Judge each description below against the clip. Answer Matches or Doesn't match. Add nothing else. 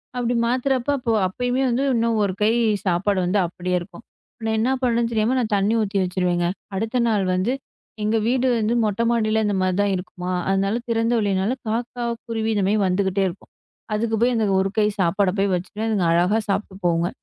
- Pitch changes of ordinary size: Matches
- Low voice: Doesn't match